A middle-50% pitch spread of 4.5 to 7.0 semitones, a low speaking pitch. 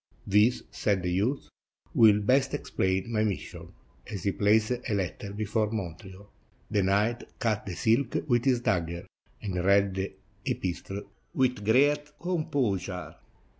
No: average, 3.9 semitones; low, 105 Hz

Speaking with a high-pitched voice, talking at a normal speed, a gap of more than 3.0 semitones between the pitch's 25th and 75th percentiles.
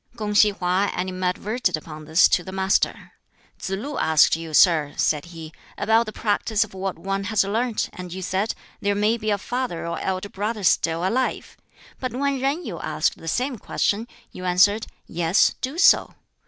Yes: high, 195 Hz; average, 180 wpm; average, 3.9 semitones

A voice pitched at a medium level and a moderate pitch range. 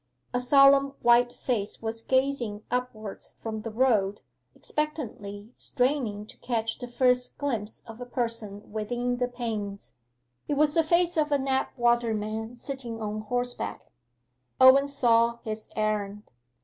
No: high, 240 Hz; average, 3.4 semitones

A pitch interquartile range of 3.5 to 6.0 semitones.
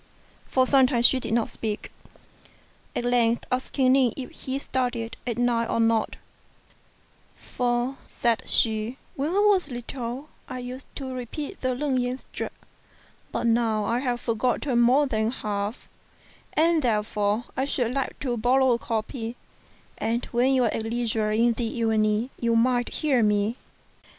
No: narrow, 2.4 semitones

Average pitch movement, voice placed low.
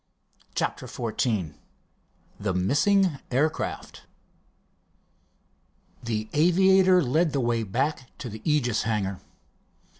No: wide, 6.5 semitones; low, 125 Hz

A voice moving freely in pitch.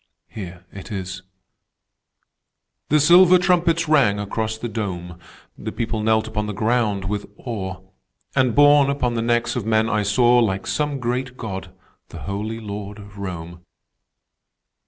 No: average, 4.0 semitones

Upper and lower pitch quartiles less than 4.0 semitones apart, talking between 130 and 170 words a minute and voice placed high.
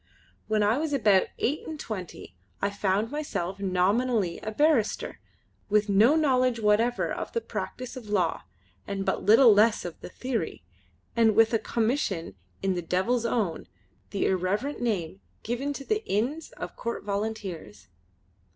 No: average, 4.4 semitones; average, 150 wpm; high, 215 Hz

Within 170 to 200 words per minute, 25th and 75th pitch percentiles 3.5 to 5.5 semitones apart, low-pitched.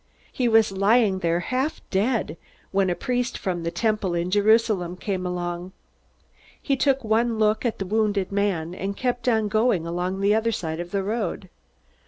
No: average, 175 wpm; average, 3.8 semitones; high, 200 Hz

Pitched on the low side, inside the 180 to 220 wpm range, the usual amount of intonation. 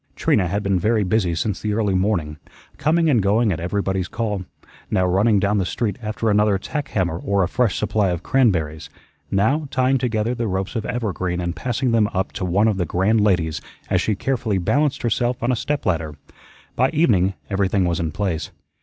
Yes: low, 100 Hz; average, 200 wpm; average, 4.0 semitones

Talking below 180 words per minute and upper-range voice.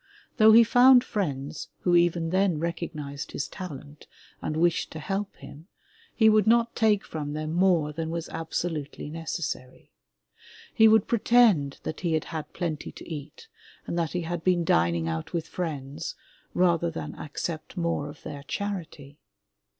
No: average, 160 wpm; medium, 165 Hz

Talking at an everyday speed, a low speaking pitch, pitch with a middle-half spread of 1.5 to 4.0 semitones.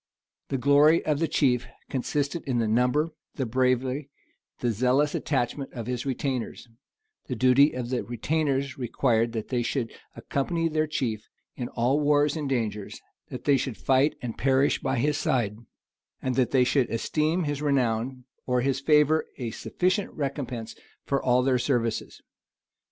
Yes: average, 160 wpm; low, 130 Hz; average, 2.9 semitones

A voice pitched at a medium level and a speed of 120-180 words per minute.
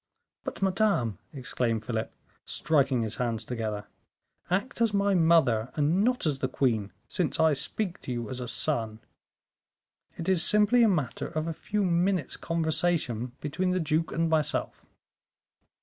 Yes: medium, 155 Hz; average, 150 wpm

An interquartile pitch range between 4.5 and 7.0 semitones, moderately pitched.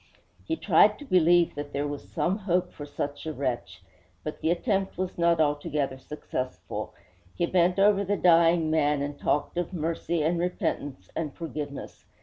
No: average, 3.5 semitones; medium, 165 Hz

